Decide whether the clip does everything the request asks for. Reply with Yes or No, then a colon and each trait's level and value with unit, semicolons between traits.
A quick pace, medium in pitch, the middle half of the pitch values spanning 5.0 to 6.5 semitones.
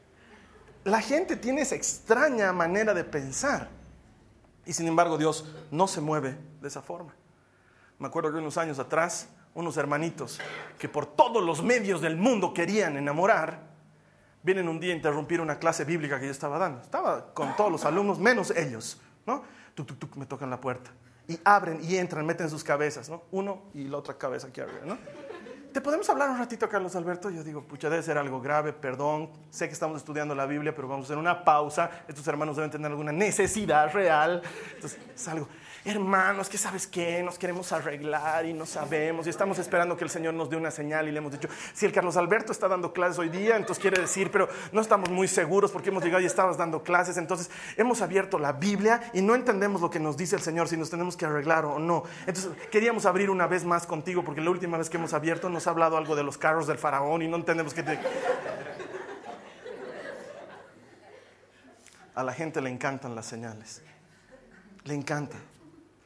No: fast, 200 wpm; medium, 165 Hz; average, 3.8 semitones